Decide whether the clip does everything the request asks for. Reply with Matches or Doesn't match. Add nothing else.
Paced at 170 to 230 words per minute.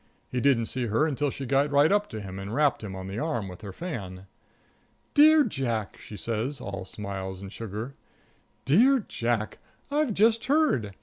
Matches